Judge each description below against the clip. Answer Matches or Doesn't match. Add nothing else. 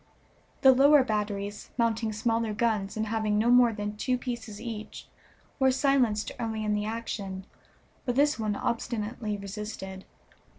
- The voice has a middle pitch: Doesn't match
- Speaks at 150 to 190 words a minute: Doesn't match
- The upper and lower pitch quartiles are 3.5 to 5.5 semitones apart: Doesn't match